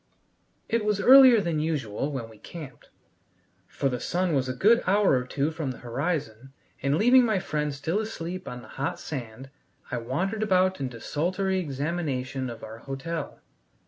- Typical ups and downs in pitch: No, wide, 6.2 semitones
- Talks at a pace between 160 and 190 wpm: Yes, average, 170 wpm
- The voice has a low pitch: No, medium, 150 Hz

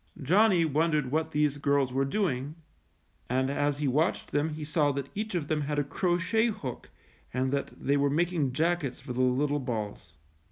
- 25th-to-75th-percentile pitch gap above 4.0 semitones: No, average, 3.1 semitones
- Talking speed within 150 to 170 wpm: No, average, 185 wpm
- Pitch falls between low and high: Yes, medium, 145 Hz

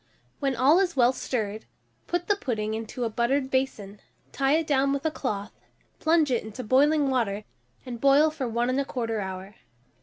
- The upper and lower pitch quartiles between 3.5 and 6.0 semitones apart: Yes, average, 4.2 semitones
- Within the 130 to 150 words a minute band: No, average, 175 wpm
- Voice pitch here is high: Yes, very high, 260 Hz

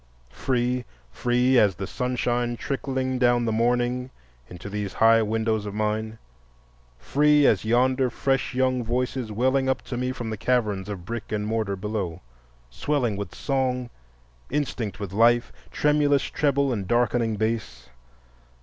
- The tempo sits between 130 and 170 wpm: Yes, average, 140 wpm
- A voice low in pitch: Yes, low, 120 Hz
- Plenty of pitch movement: No, average, 3.3 semitones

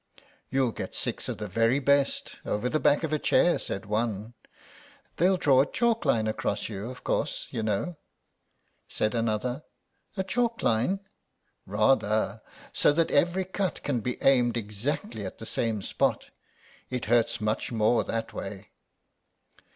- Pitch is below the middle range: Yes, low, 120 Hz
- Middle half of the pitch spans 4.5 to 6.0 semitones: Yes, average, 5.3 semitones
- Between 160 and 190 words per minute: No, average, 150 wpm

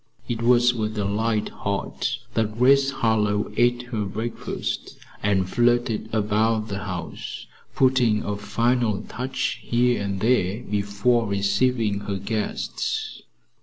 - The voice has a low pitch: Yes, low, 110 Hz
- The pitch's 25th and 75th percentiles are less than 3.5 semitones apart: Yes, average, 2.9 semitones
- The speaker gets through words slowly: Yes, slow, 125 wpm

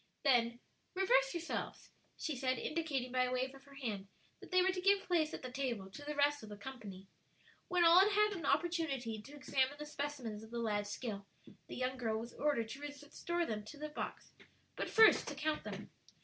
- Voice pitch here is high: Yes, very high, 275 Hz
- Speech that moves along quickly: Yes, fast, 210 wpm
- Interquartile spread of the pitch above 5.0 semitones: Yes, wide, 5.4 semitones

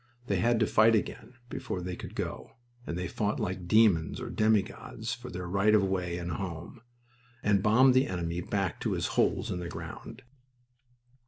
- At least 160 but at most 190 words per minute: Yes, average, 180 wpm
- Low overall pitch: Yes, low, 100 Hz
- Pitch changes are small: No, average, 3.8 semitones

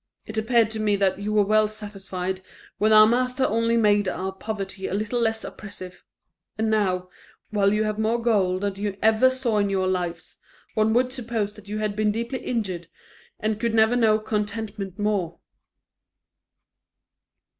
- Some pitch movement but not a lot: No, narrow, 2.0 semitones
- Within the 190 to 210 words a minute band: No, average, 165 wpm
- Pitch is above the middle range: Yes, high, 215 Hz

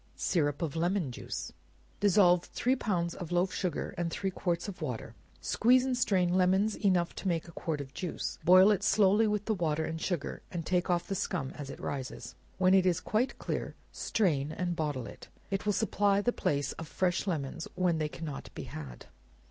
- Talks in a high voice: No, medium, 180 Hz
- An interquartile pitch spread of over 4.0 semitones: No, average, 3.6 semitones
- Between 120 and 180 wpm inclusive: No, average, 195 wpm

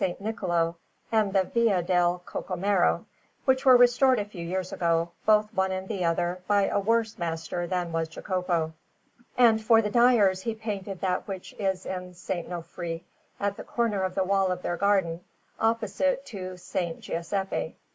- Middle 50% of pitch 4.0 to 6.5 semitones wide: No, average, 3.5 semitones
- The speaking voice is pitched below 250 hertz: Yes, high, 190 Hz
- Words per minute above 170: No, average, 165 wpm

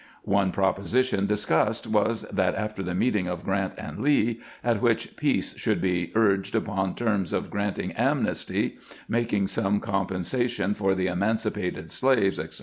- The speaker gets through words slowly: No, average, 145 wpm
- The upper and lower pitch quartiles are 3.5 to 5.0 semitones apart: No, average, 2.8 semitones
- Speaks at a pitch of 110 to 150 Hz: No, low, 100 Hz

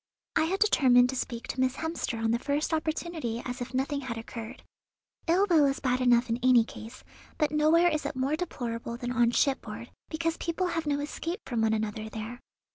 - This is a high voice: Yes, very high, 260 Hz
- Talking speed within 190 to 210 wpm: Yes, average, 200 wpm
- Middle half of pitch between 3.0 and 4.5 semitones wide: No, average, 5.0 semitones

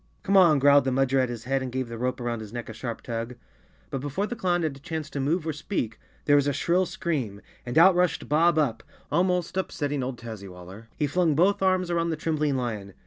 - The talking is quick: Yes, fast, 245 wpm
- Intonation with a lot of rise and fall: Yes, wide, 5.7 semitones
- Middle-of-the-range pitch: Yes, medium, 145 Hz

